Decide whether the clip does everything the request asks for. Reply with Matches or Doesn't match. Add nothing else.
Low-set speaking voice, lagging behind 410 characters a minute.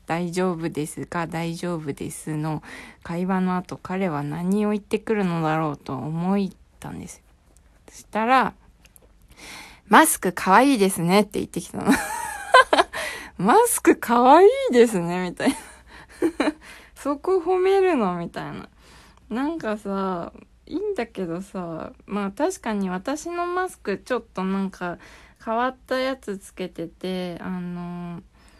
Doesn't match